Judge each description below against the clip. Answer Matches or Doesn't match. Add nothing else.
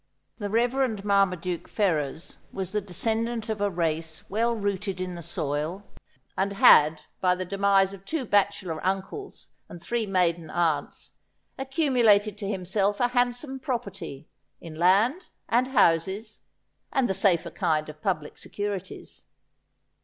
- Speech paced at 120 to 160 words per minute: Matches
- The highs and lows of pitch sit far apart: Doesn't match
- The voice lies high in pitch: Matches